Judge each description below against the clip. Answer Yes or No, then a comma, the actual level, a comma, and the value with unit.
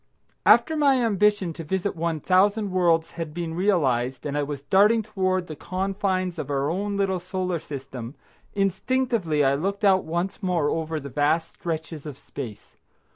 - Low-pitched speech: No, medium, 175 Hz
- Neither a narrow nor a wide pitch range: Yes, average, 4.5 semitones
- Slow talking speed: No, average, 165 wpm